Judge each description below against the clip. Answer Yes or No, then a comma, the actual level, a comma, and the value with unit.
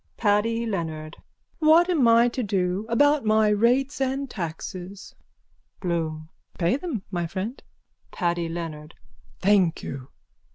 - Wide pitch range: Yes, wide, 5.7 semitones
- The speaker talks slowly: Yes, slow, 120 wpm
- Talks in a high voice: Yes, high, 205 Hz